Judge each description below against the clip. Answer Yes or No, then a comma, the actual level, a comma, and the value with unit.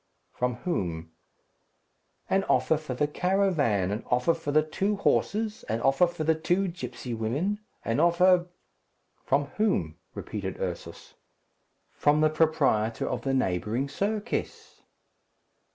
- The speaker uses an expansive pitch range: Yes, wide, 7.7 semitones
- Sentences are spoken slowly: Yes, slow, 130 wpm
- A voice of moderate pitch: Yes, medium, 150 Hz